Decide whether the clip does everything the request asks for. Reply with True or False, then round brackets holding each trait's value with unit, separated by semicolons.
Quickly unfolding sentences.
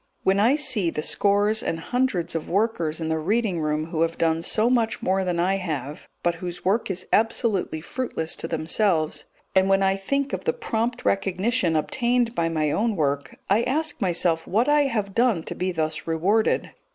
False (190 wpm)